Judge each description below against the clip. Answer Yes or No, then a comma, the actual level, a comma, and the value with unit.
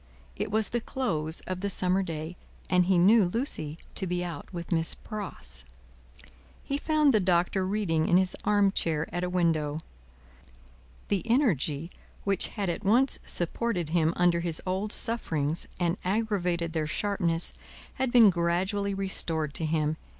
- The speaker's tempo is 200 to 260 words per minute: No, average, 155 wpm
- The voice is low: No, medium, 180 Hz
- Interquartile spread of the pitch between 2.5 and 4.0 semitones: Yes, average, 3.7 semitones